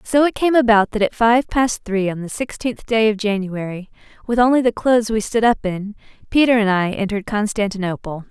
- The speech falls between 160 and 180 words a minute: No, average, 200 wpm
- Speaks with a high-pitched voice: Yes, high, 220 Hz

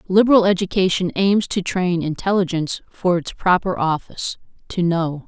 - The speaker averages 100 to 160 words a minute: Yes, slow, 135 wpm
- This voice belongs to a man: No, female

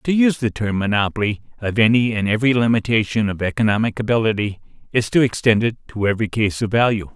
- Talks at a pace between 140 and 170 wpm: No, average, 185 wpm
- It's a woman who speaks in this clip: No, male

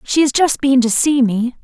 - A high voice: Yes, very high, 260 Hz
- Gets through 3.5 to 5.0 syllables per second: Yes, 4.7 syllables/s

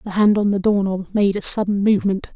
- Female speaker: Yes, female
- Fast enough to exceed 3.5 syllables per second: Yes, 6.1 syllables/s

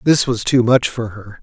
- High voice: No, low, 120 Hz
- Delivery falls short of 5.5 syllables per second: Yes, 4.6 syllables/s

